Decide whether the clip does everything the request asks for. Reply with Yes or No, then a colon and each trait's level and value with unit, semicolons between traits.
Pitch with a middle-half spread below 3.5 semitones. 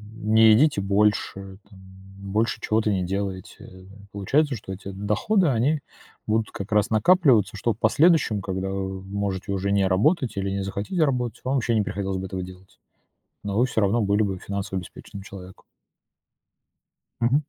Yes: average, 3.1 semitones